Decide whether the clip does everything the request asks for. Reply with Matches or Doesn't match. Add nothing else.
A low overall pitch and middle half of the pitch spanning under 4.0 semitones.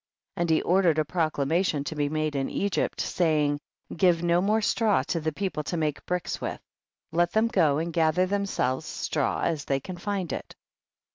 Doesn't match